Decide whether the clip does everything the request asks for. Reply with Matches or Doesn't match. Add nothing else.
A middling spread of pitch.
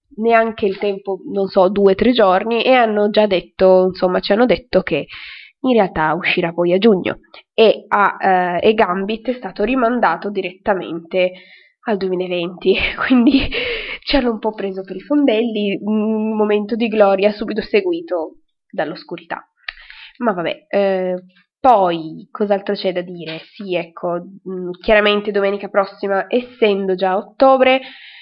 Matches